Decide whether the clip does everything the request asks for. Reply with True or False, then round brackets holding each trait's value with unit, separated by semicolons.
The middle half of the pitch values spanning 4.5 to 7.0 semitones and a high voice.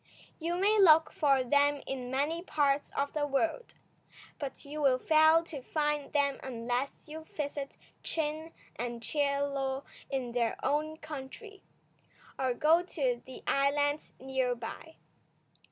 False (2.8 semitones; 285 Hz)